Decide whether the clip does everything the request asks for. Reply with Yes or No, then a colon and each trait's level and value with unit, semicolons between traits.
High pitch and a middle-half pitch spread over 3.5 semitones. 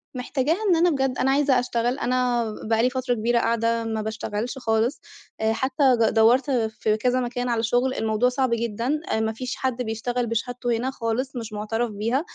No: high, 240 Hz; narrow, 2.4 semitones